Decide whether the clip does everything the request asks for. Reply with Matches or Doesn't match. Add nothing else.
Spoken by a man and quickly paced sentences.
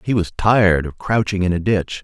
Matches